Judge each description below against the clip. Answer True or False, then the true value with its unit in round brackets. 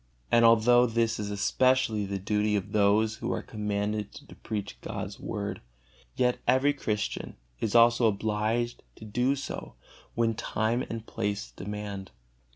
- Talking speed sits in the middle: True (145 wpm)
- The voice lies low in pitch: True (110 Hz)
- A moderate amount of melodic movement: False (2.1 semitones)